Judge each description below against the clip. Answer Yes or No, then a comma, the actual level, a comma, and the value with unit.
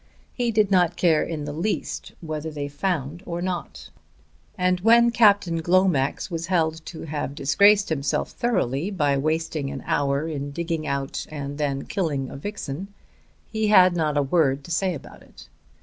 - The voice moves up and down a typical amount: Yes, average, 4.5 semitones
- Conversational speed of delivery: Yes, average, 165 wpm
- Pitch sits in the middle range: Yes, medium, 160 Hz